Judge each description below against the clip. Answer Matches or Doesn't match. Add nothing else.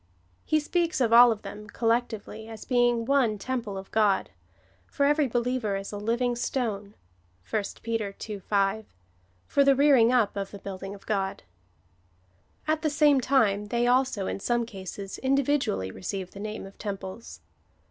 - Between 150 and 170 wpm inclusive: Matches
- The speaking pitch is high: Matches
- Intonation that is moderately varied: Matches